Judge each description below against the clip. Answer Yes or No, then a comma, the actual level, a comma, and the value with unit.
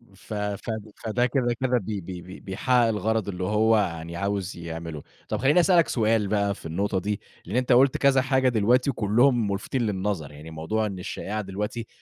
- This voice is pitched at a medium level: No, low, 105 Hz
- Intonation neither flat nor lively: Yes, average, 4.2 semitones